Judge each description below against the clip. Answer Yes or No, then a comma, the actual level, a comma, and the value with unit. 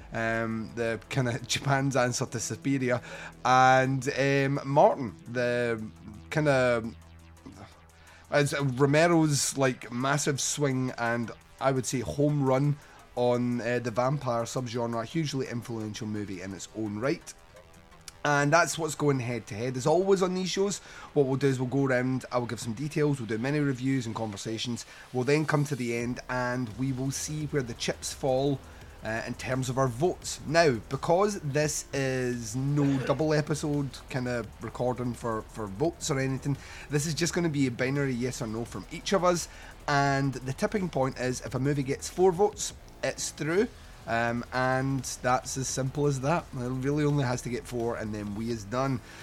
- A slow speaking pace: No, average, 185 wpm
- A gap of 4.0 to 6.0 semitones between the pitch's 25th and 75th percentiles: No, average, 3.5 semitones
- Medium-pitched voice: No, low, 130 Hz